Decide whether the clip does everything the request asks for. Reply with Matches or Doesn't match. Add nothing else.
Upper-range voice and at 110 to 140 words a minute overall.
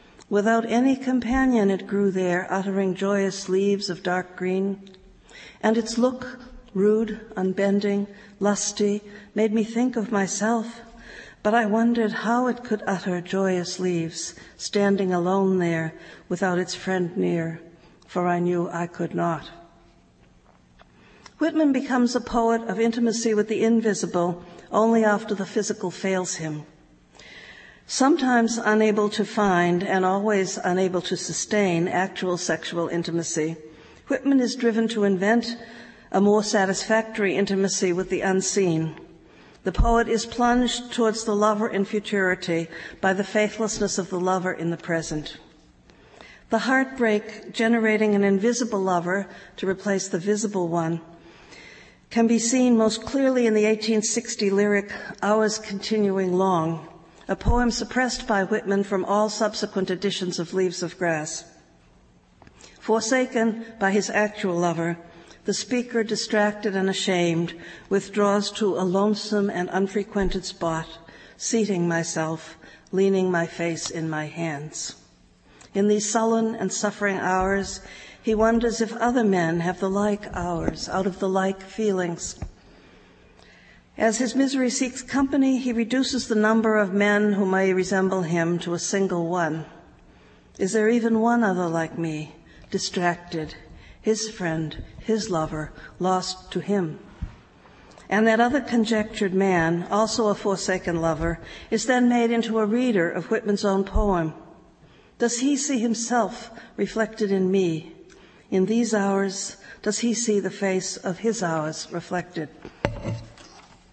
Matches